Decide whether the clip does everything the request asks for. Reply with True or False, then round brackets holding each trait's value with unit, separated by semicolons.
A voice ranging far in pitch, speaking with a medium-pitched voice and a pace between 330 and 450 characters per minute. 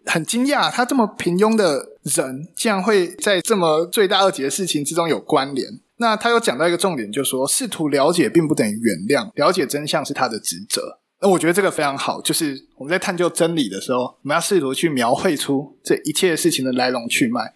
True (6.3 semitones; 170 Hz; 340 characters per minute)